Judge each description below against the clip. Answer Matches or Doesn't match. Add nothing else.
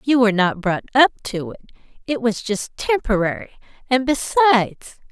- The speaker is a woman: Matches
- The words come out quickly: Doesn't match